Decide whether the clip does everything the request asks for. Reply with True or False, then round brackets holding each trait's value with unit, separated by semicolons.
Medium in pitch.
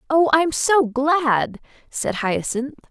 False (280 Hz)